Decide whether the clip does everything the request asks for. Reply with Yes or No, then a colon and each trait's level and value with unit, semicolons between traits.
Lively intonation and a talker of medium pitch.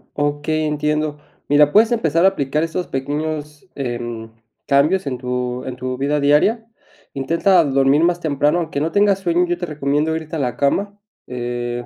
No: average, 3.7 semitones; medium, 150 Hz